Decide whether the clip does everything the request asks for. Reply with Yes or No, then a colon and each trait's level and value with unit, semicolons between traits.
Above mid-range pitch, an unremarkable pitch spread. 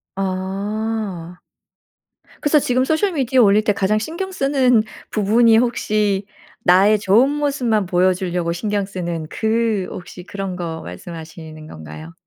Yes: high, 205 Hz; average, 4.5 semitones